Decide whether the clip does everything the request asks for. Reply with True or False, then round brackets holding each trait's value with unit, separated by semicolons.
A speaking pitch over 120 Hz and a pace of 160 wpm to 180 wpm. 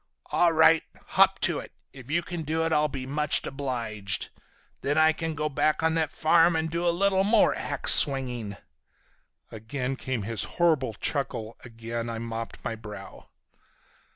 True (140 Hz; 165 wpm)